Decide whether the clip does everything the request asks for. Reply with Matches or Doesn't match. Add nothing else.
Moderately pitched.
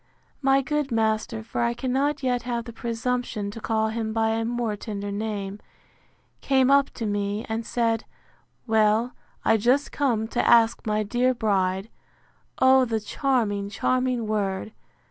Doesn't match